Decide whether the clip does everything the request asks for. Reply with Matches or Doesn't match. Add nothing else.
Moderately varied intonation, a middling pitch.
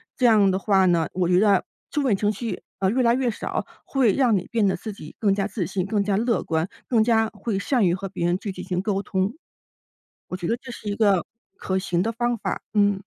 Doesn't match